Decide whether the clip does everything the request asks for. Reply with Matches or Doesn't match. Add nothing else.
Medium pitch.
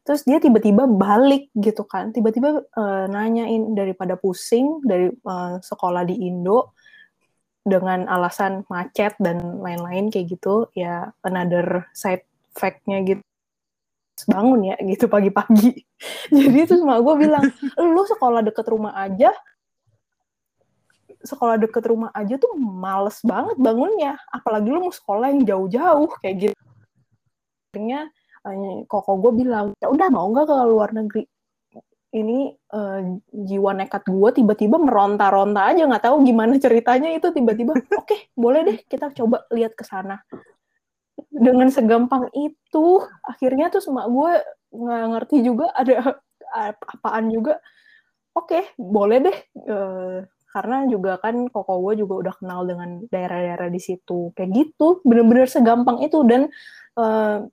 Doesn't match